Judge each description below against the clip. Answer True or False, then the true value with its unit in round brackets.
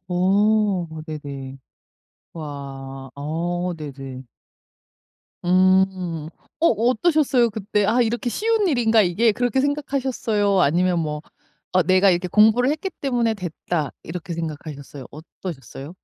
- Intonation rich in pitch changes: True (6.6 semitones)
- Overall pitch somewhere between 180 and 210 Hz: True (185 Hz)